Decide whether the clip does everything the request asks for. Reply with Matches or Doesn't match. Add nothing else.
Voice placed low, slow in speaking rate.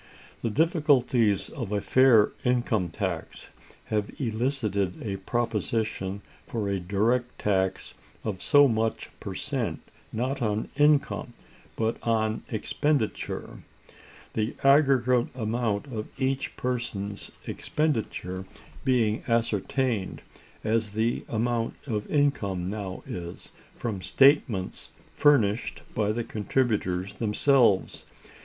Matches